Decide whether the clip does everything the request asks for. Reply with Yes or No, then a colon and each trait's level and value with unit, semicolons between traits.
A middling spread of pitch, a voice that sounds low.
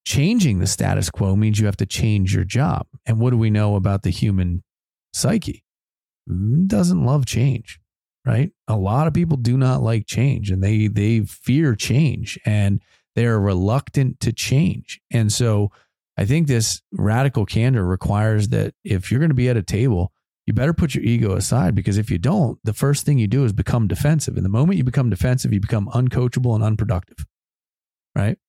Yes: average, 4.4 semitones; low, 115 Hz